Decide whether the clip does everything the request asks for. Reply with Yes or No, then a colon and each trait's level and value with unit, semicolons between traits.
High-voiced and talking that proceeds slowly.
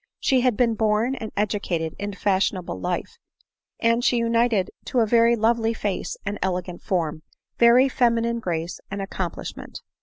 No: high, 215 Hz; average, 155 wpm